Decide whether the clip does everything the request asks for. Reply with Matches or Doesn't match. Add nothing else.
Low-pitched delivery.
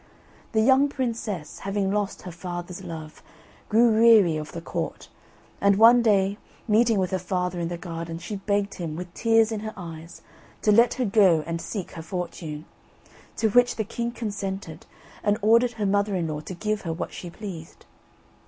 Doesn't match